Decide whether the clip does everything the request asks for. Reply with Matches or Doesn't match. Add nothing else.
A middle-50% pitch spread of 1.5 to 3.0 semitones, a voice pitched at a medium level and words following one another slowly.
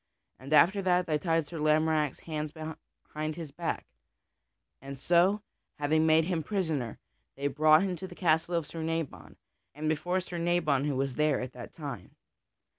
Doesn't match